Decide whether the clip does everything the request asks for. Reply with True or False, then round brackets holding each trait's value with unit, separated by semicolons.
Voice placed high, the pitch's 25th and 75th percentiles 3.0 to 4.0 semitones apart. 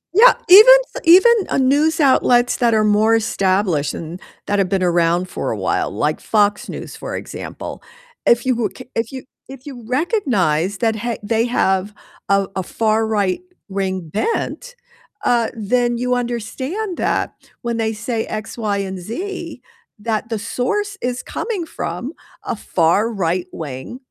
False (225 Hz; 4.7 semitones)